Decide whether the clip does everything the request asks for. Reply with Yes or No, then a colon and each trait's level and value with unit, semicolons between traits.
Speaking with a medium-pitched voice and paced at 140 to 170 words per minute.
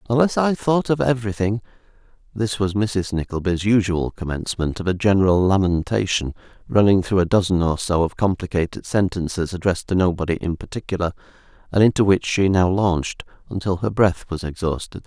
No: very low, 95 Hz; average, 160 wpm